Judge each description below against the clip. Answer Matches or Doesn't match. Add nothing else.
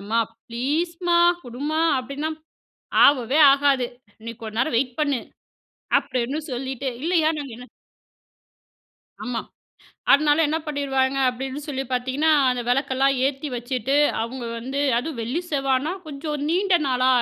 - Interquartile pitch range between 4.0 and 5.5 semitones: Doesn't match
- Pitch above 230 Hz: Matches